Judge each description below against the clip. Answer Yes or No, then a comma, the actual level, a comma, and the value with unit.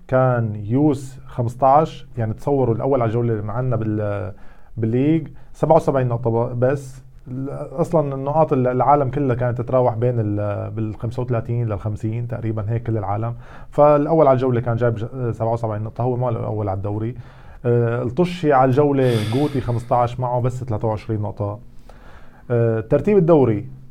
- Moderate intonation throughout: Yes, average, 3.0 semitones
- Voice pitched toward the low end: Yes, low, 125 Hz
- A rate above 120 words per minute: Yes, average, 130 wpm